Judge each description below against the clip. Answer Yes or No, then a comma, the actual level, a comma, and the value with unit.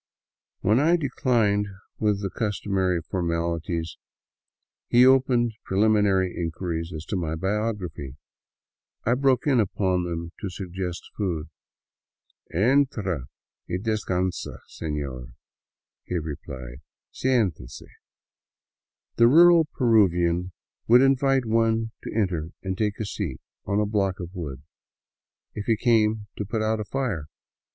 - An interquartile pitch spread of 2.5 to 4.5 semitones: No, average, 4.9 semitones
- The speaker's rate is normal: No, slow, 130 wpm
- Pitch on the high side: No, low, 100 Hz